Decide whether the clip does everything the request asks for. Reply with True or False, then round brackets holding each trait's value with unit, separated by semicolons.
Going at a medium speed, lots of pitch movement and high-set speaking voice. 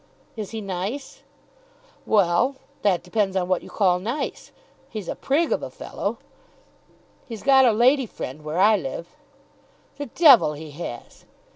True (150 wpm; 5.9 semitones; 205 Hz)